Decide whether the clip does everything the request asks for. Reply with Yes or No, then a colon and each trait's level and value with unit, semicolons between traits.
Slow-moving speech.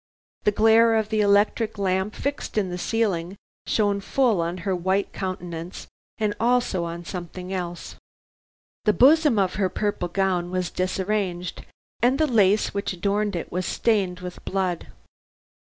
No: average, 150 wpm